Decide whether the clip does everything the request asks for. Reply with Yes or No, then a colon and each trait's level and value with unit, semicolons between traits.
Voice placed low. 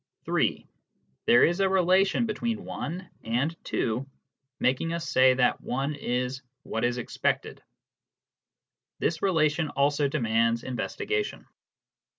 No: medium, 145 Hz